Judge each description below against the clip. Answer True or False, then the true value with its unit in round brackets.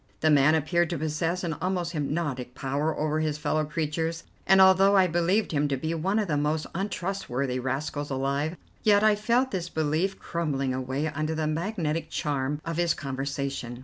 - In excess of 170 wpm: True (180 wpm)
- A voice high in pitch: False (155 Hz)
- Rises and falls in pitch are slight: False (3.3 semitones)